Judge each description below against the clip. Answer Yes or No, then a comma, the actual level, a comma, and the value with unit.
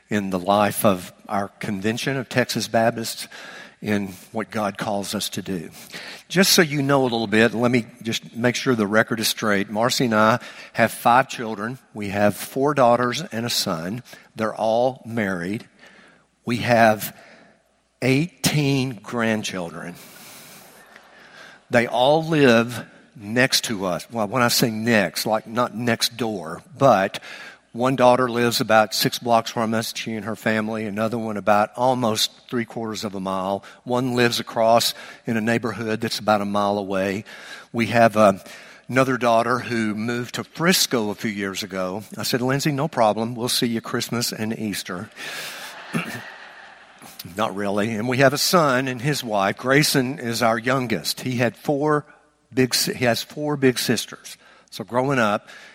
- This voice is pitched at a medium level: No, low, 115 Hz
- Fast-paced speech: No, average, 160 wpm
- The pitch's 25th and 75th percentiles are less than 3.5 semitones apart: Yes, average, 3.0 semitones